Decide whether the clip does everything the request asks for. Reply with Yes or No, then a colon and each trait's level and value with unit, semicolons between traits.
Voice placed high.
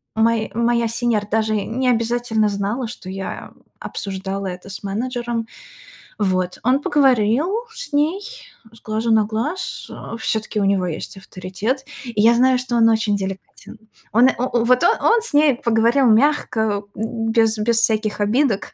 Yes: high, 225 Hz